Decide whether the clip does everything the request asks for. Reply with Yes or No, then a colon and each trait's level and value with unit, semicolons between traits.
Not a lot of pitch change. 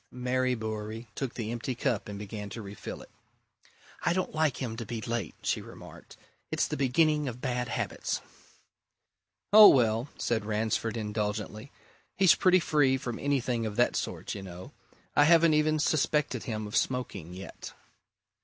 No: average, 4.7 semitones